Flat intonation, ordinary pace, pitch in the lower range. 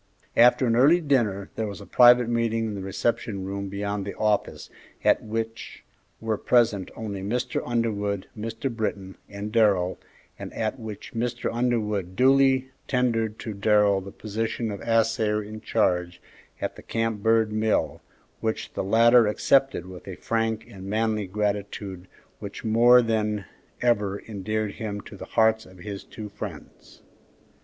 Yes: narrow, 2.3 semitones; average, 150 wpm; low, 110 Hz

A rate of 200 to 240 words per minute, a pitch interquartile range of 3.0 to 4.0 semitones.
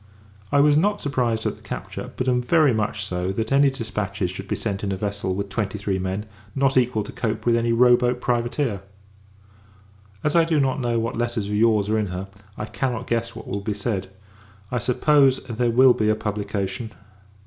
Yes: fast, 205 wpm; average, 3.6 semitones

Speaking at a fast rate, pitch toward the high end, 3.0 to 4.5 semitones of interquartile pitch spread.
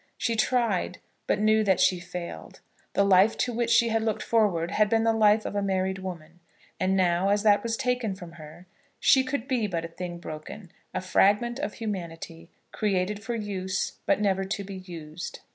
No: average, 195 wpm; high, 200 Hz; average, 3.6 semitones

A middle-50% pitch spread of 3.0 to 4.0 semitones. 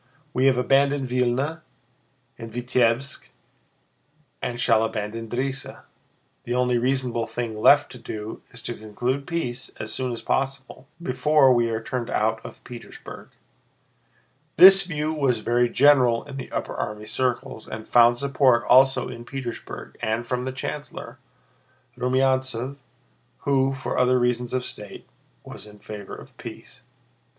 No: narrow, 2.4 semitones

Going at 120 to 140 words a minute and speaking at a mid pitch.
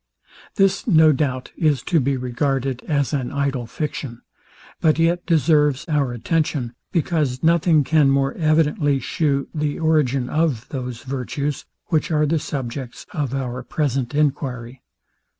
Yes: slow, 135 wpm; medium, 145 Hz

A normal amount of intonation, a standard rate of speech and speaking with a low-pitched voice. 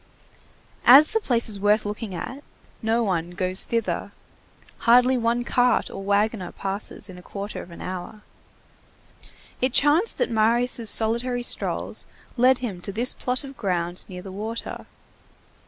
No: average, 4.0 semitones; average, 150 wpm; high, 225 Hz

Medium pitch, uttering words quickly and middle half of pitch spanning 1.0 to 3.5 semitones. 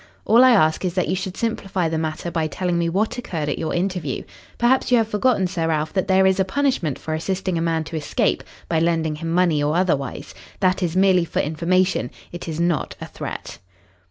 Yes: medium, 175 Hz; fast, 215 wpm; average, 3.0 semitones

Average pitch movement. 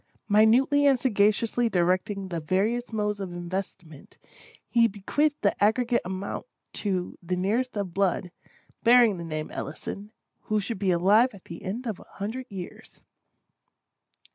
Yes: average, 4.0 semitones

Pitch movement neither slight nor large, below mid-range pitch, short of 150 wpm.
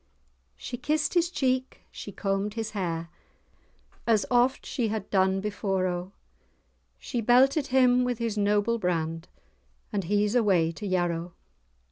No: average, 4.8 semitones; high, 210 Hz; slow, 135 wpm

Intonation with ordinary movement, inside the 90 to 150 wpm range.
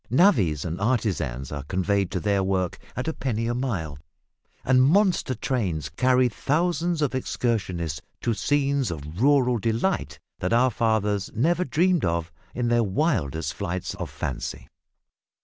No: wide, 6.6 semitones; average, 145 wpm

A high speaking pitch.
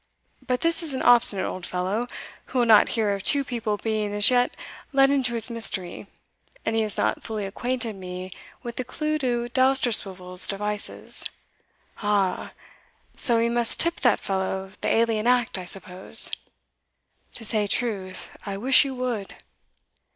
Yes: high, 225 Hz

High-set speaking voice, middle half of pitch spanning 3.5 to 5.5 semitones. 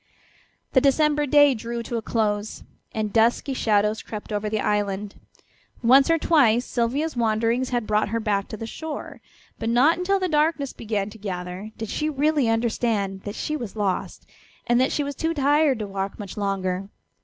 Yes: high, 230 Hz; average, 5.2 semitones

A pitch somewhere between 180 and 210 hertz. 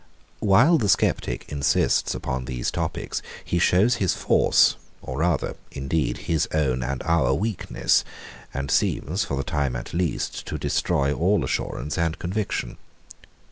No: very low, 80 Hz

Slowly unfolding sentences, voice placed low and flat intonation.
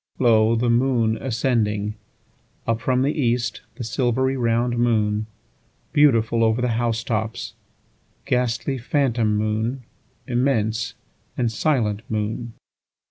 Yes: slow, 95 wpm; low, 115 Hz; narrow, 2.2 semitones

